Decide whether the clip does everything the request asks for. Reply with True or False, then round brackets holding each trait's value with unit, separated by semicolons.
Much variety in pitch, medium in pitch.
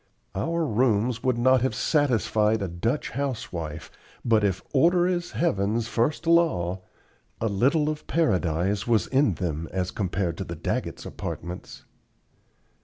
False (7.1 semitones; 115 Hz)